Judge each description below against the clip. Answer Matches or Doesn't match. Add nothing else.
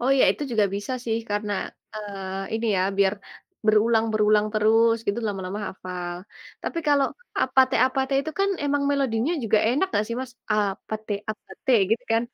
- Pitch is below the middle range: Doesn't match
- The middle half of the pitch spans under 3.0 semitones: Doesn't match